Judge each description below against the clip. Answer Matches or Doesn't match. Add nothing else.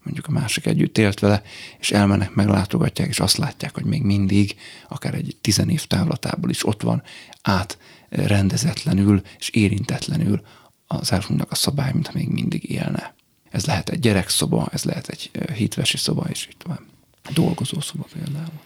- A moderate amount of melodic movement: Doesn't match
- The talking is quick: Matches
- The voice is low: Matches